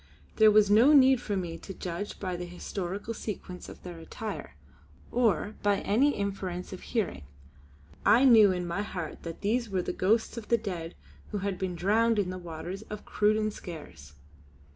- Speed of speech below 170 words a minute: No, average, 185 wpm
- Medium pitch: No, high, 200 Hz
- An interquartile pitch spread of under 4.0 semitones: Yes, average, 3.4 semitones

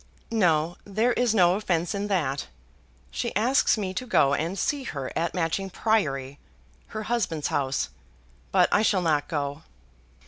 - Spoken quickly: No, average, 150 wpm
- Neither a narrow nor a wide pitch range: No, wide, 6.0 semitones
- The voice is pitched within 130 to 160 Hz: No, medium, 180 Hz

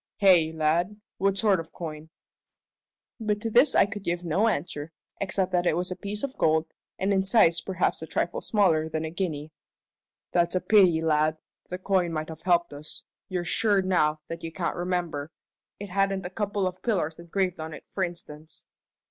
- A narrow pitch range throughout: No, average, 3.4 semitones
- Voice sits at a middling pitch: Yes, medium, 175 Hz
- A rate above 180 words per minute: Yes, average, 190 wpm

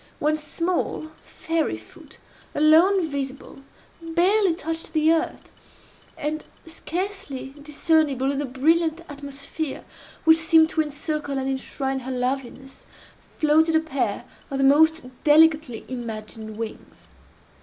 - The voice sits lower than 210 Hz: No, very high, 305 Hz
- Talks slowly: Yes, slow, 115 wpm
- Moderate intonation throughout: Yes, average, 3.2 semitones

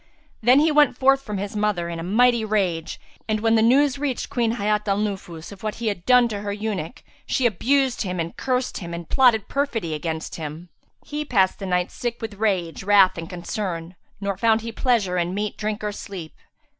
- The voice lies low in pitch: No, high, 210 Hz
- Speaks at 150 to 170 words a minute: No, fast, 205 wpm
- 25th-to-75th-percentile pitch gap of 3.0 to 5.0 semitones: Yes, average, 4.7 semitones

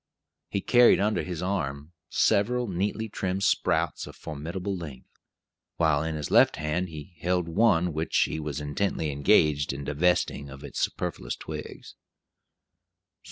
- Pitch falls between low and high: No, very low, 85 Hz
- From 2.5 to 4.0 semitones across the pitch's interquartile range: No, average, 4.6 semitones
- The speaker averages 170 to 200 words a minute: No, average, 145 wpm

